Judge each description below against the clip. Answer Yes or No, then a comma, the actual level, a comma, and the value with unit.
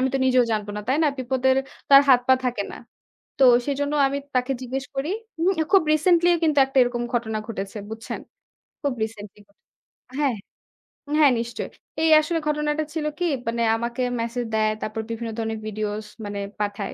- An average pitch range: Yes, average, 4.3 semitones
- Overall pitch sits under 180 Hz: No, high, 245 Hz